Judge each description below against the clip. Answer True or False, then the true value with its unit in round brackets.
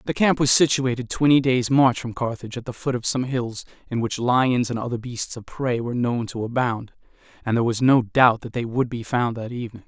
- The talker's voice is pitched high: False (120 Hz)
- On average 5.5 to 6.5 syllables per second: True (5.6 syllables/s)